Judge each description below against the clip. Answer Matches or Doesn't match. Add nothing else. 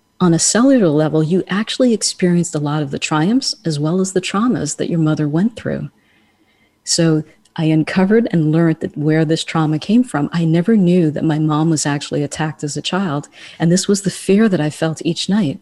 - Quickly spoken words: Matches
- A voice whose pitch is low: Doesn't match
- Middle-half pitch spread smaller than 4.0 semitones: Matches